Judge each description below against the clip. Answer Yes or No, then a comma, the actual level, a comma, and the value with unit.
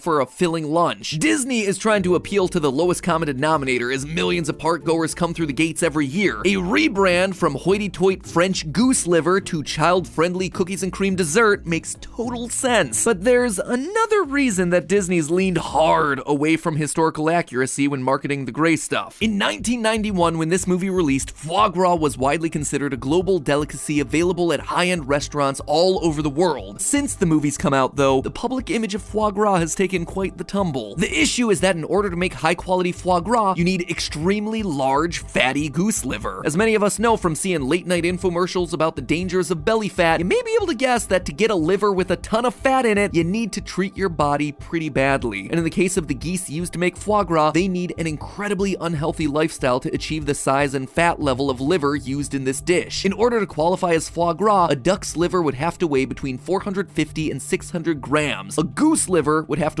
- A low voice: No, medium, 175 Hz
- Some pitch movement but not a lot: Yes, average, 4.1 semitones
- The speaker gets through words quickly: Yes, fast, 220 wpm